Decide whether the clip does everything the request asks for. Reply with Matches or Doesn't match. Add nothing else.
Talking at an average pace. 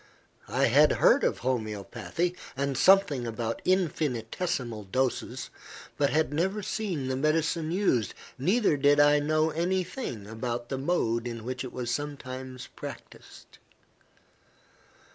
Doesn't match